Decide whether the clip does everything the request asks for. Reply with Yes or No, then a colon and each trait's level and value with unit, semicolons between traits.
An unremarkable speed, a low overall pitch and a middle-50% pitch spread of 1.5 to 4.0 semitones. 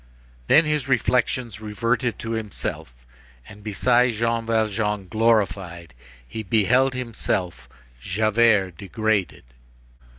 No: slow, 95 wpm; low, 110 Hz; average, 2.7 semitones